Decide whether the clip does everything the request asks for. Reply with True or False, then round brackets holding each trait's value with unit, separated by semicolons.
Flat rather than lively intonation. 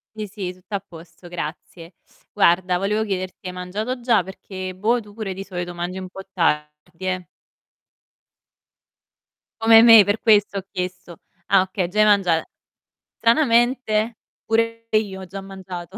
False (3.0 semitones)